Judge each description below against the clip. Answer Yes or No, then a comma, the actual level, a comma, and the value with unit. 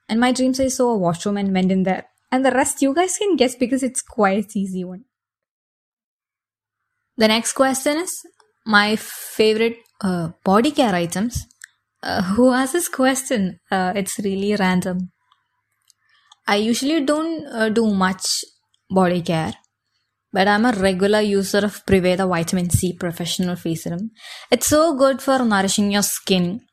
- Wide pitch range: Yes, wide, 5.7 semitones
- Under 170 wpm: Yes, average, 155 wpm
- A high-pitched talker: Yes, high, 210 Hz